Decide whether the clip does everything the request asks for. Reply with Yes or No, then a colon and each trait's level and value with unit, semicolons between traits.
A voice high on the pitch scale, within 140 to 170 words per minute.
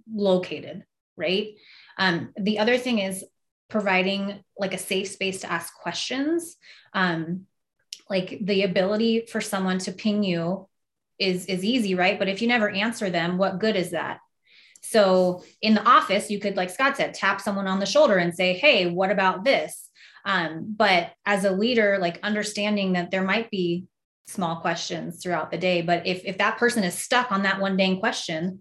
No: high, 195 Hz; average, 180 wpm